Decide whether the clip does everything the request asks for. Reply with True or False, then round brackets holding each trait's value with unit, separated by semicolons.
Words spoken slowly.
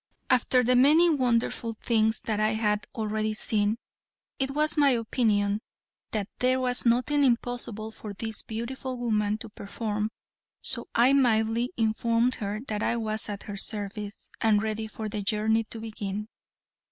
False (150 wpm)